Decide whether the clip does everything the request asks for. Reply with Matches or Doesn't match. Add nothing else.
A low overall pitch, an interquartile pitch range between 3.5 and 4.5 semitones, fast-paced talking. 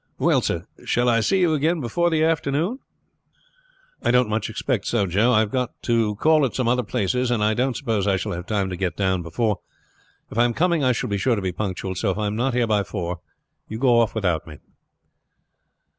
Matches